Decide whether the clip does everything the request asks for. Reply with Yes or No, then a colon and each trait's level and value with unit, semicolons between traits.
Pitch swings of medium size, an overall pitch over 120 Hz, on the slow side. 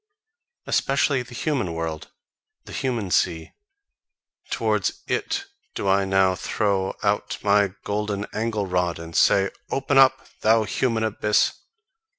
No: average, 3.7 semitones; low, 105 Hz; slow, 125 wpm